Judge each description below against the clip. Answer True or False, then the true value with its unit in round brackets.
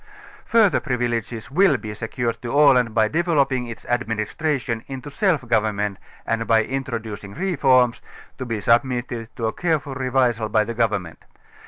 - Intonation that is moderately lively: True (3.3 semitones)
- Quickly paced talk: False (150 wpm)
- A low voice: True (120 Hz)